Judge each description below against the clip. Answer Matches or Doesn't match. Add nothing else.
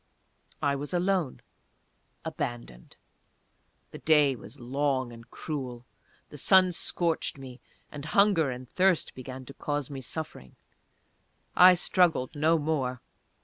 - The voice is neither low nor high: Matches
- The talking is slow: Matches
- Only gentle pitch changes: Doesn't match